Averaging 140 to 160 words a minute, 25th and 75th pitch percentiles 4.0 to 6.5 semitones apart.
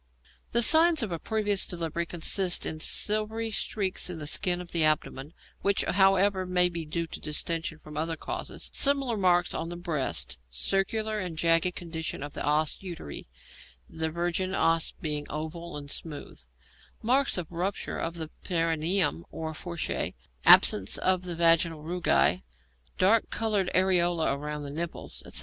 No: average, 155 wpm; average, 3.2 semitones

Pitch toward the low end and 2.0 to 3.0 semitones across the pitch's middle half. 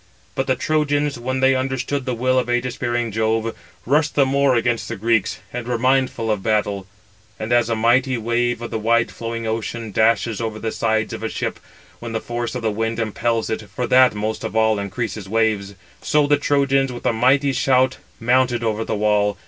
Yes: low, 120 Hz; average, 2.7 semitones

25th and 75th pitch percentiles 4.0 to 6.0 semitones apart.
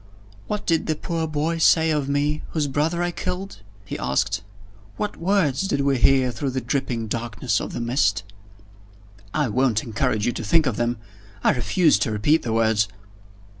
Yes: average, 5.3 semitones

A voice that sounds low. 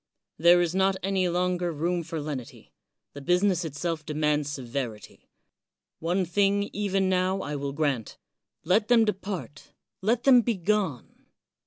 No: medium, 175 Hz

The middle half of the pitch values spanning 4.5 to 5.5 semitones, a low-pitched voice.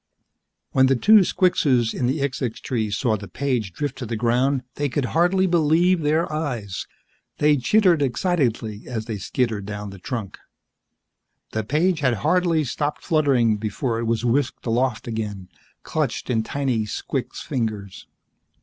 Yes: average, 5.2 semitones; low, 125 Hz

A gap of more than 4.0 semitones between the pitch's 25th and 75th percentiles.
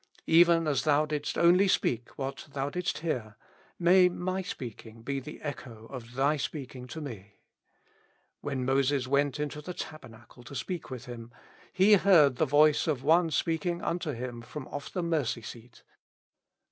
Yes: average, 4.7 semitones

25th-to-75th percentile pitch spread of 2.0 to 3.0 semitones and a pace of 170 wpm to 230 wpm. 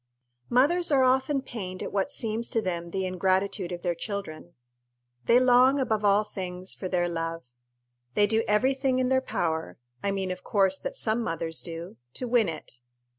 No: wide, 5.6 semitones; average, 185 wpm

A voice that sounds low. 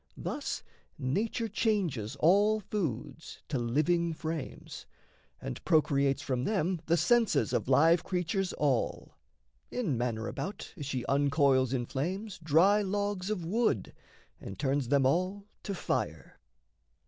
No: medium, 160 Hz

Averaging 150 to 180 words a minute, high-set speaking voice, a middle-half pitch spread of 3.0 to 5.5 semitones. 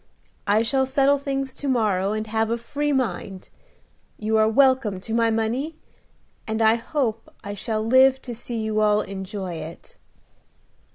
Yes: average, 160 wpm; high, 225 Hz; average, 3.7 semitones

